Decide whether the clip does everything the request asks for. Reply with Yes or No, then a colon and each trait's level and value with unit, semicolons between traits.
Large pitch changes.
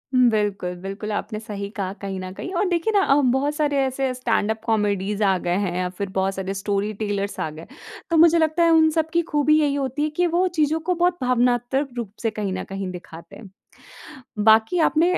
Yes: wide, 7.4 semitones